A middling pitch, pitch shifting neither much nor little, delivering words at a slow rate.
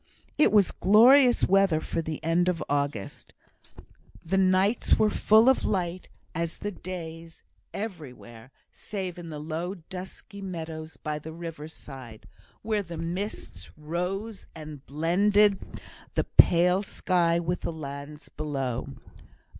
Yes: medium, 170 Hz; average, 4.0 semitones; slow, 130 wpm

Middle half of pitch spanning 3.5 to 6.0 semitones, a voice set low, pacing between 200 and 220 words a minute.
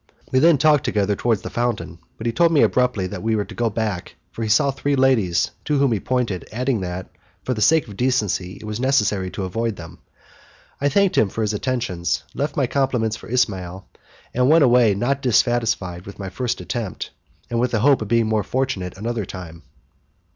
Yes: average, 4.6 semitones; low, 115 Hz; fast, 205 wpm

